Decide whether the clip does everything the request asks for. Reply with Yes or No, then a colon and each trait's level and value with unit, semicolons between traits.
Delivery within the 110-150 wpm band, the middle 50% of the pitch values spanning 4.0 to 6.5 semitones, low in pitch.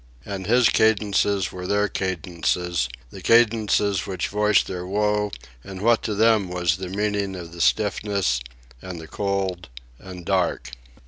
No: average, 145 wpm; narrow, 2.6 semitones; very low, 95 Hz